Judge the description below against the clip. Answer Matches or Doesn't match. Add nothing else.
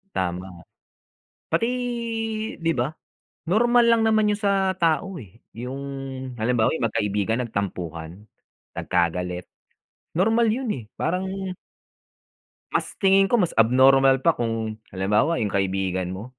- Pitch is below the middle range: Matches